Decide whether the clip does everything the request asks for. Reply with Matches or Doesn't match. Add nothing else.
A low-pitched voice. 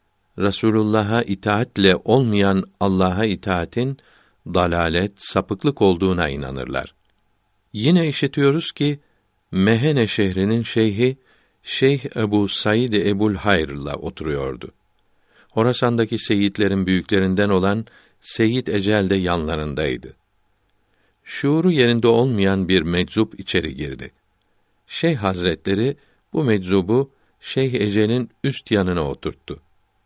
Matches